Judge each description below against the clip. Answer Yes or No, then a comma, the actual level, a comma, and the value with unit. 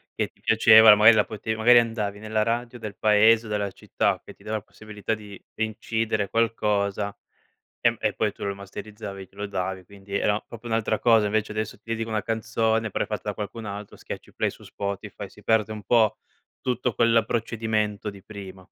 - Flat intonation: Yes, narrow, 1.7 semitones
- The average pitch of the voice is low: Yes, low, 110 Hz